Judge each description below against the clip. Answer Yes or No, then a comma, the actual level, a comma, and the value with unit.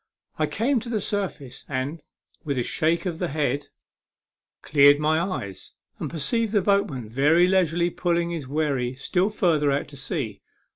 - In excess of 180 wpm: No, average, 165 wpm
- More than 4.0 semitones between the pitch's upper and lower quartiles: Yes, average, 4.5 semitones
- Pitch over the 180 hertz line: No, medium, 155 Hz